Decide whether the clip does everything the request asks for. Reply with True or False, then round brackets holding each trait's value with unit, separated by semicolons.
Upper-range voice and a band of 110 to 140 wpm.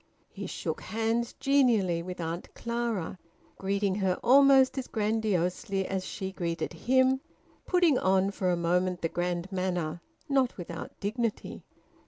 True (195 Hz; 135 wpm)